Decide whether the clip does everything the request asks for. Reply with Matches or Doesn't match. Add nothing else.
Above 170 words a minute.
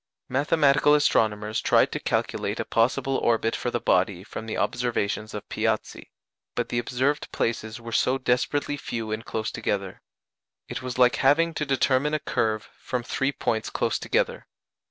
Doesn't match